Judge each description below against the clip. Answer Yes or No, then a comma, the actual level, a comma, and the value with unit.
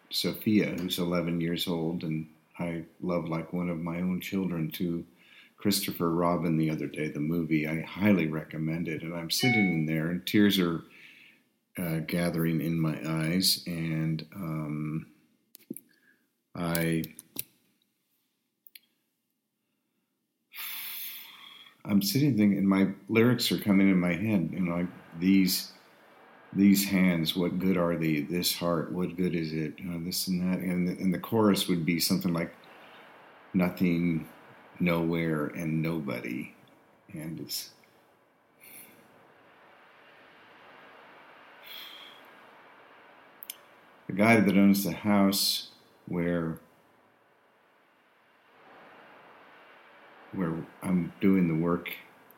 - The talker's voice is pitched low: Yes, very low, 85 Hz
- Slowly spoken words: Yes, slow, 115 wpm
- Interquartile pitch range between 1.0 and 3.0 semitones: Yes, narrow, 2.5 semitones